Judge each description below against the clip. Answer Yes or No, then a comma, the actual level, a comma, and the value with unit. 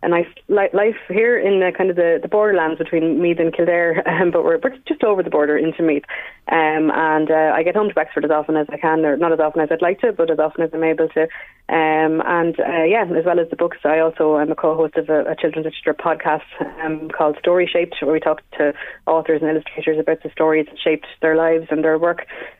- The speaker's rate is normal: No, fast, 245 wpm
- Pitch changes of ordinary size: No, narrow, 1.6 semitones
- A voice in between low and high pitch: Yes, medium, 160 Hz